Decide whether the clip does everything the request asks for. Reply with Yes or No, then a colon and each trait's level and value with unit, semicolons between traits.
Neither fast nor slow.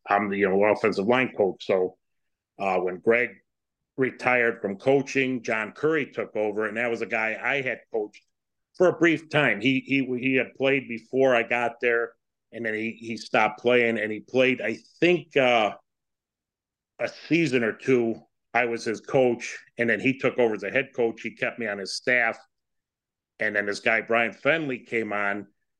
Yes: average, 190 wpm